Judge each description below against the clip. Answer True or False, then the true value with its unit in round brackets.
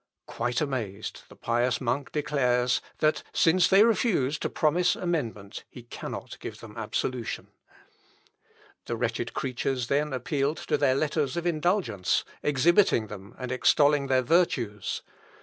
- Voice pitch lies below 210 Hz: True (135 Hz)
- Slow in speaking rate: True (130 wpm)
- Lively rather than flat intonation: False (4.3 semitones)